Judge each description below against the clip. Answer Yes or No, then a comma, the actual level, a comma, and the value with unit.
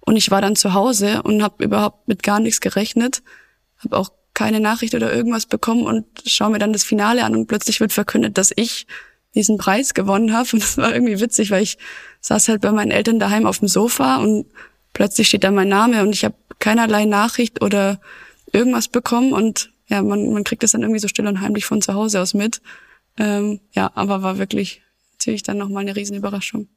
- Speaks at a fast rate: Yes, fast, 210 wpm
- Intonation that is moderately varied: No, narrow, 2.2 semitones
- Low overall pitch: No, high, 215 Hz